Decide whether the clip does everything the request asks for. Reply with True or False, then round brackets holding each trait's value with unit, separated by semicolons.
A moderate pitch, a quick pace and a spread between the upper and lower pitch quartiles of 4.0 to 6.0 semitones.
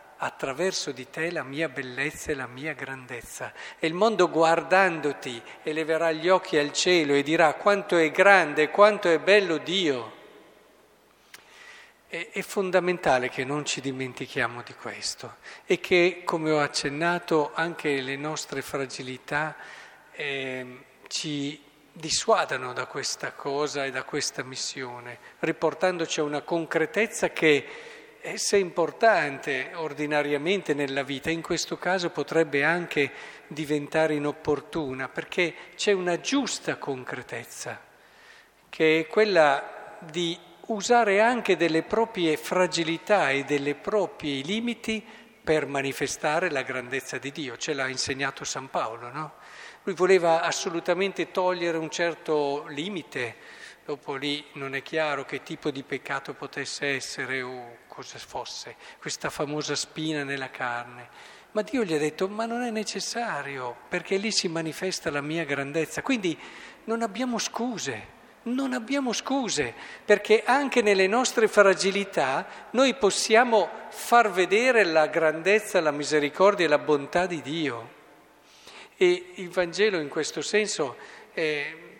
False (160 Hz; 130 wpm; 5.5 semitones)